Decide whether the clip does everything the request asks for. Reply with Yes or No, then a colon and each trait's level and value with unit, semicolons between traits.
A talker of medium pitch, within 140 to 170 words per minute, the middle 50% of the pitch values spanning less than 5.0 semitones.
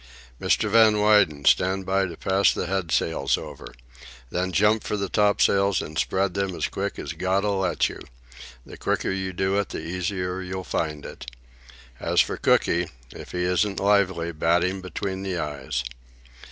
No: very low, 95 Hz; average, 165 wpm; narrow, 2.6 semitones